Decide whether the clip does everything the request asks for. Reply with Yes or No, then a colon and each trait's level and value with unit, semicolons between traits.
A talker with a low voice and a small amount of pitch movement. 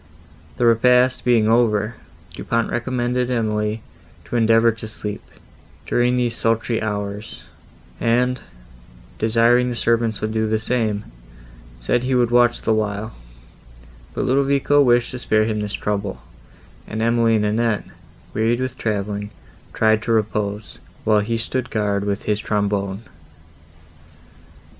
Yes: low, 115 Hz; narrow, 2.2 semitones